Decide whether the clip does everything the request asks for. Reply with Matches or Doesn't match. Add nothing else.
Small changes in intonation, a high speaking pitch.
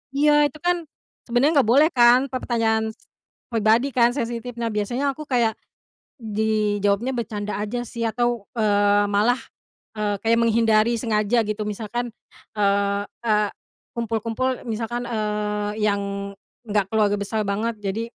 Matches